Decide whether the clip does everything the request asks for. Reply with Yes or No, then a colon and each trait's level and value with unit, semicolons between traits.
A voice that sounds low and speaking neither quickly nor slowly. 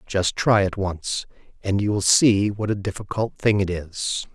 Yes: low, 100 Hz; average, 195 wpm